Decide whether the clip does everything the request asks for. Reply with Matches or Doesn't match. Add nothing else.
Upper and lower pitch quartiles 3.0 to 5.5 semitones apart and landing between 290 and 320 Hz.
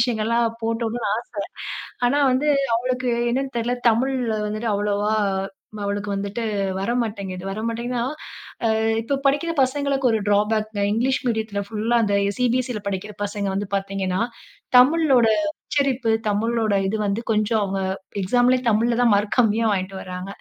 Doesn't match